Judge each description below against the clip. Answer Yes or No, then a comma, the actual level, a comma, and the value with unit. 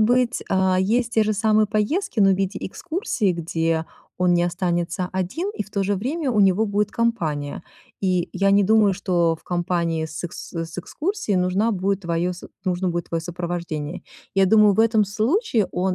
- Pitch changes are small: No, average, 3.6 semitones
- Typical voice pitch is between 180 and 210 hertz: Yes, high, 190 Hz